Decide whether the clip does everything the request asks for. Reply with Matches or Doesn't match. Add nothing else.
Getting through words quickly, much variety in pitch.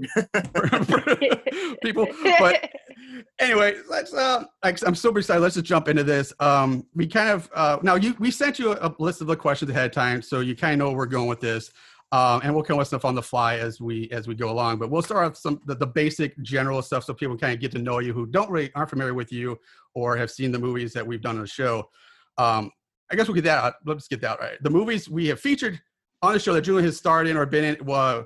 Matches